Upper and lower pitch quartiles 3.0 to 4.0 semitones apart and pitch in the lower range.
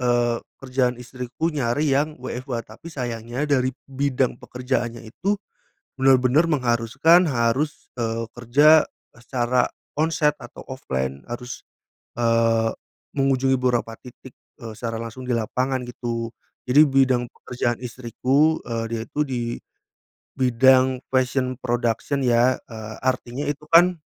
No: narrow, 2.5 semitones; low, 125 Hz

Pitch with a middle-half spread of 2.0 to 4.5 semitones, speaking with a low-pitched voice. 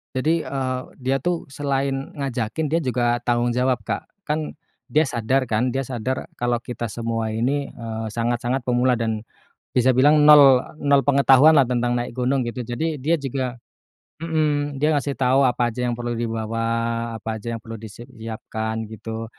Yes: average, 2.9 semitones; low, 125 Hz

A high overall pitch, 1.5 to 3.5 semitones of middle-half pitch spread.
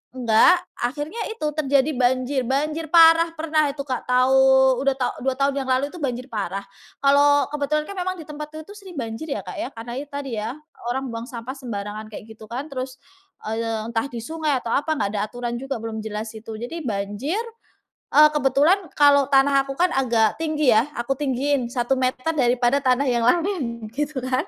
No: very high, 265 Hz; average, 3.9 semitones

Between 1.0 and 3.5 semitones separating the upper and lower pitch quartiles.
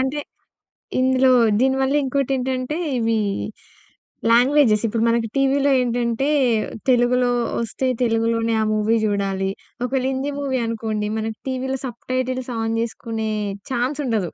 Yes: average, 2.7 semitones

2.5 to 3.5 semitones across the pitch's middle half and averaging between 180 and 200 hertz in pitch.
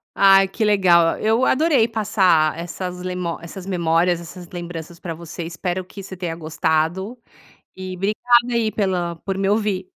Yes: average, 3.0 semitones; medium, 185 Hz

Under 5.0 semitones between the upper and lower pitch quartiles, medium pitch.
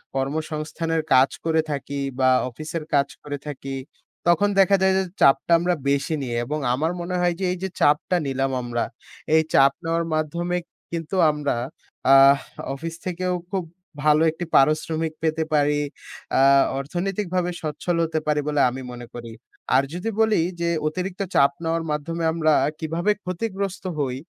Yes: average, 3.7 semitones; medium, 160 Hz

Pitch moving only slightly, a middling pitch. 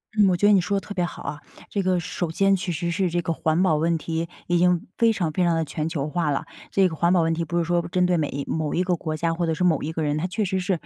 Yes: narrow, 2.1 semitones; medium, 170 Hz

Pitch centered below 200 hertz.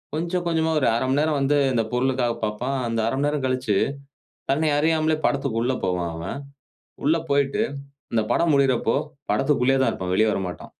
Yes: low, 135 Hz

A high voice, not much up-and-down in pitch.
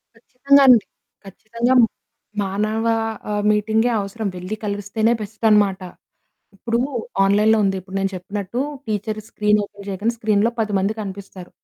Yes: high, 210 Hz; narrow, 2.1 semitones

